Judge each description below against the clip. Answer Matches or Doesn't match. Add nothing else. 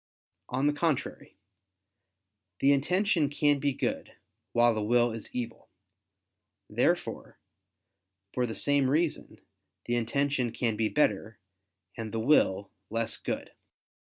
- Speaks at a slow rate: Matches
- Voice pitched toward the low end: Matches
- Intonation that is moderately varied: Matches